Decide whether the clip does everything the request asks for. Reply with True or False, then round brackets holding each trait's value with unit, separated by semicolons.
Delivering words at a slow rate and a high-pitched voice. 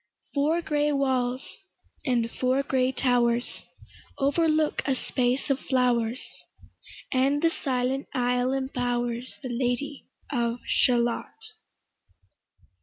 True (100 wpm; 255 Hz)